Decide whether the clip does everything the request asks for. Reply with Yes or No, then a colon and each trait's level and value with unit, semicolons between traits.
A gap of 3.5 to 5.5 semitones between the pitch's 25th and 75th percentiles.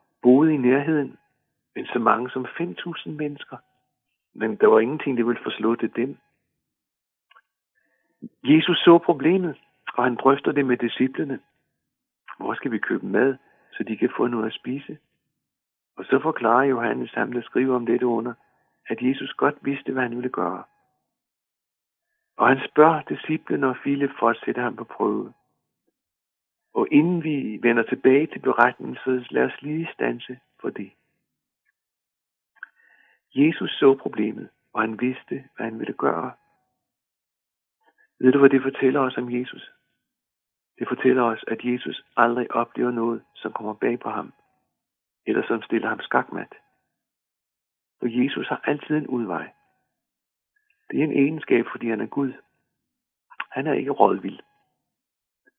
Yes: average, 3.9 semitones